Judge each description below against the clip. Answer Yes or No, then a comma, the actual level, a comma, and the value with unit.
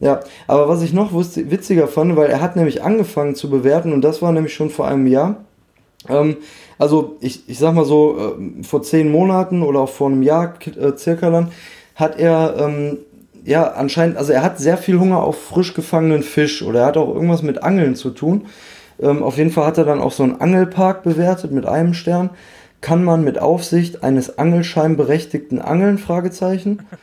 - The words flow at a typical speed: No, fast, 195 wpm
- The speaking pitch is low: No, medium, 160 Hz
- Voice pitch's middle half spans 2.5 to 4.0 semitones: Yes, average, 2.8 semitones